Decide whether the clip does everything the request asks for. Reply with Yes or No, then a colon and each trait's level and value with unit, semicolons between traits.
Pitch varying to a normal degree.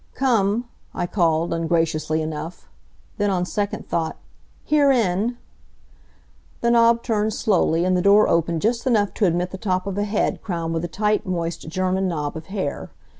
Yes: average, 4.2 semitones